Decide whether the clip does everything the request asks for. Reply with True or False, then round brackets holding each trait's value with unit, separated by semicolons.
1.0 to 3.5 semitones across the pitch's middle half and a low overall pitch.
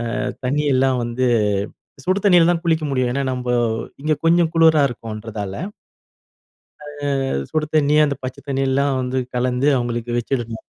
False (3.9 semitones; 130 Hz)